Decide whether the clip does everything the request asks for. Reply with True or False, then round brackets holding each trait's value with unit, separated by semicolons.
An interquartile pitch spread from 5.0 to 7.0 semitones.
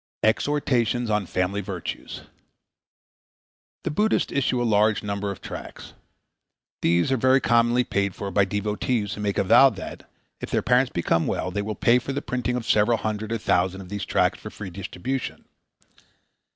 False (3.8 semitones)